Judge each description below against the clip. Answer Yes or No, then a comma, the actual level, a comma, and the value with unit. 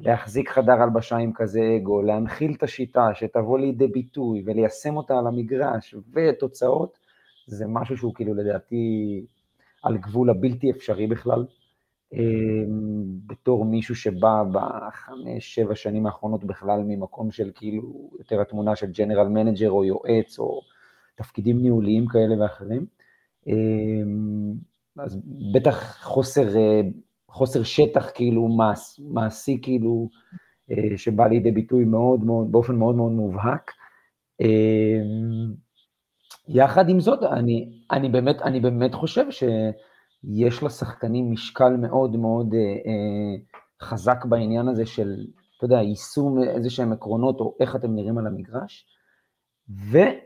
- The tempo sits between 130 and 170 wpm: No, average, 120 wpm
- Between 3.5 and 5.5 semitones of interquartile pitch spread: No, narrow, 2.5 semitones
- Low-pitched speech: Yes, low, 115 Hz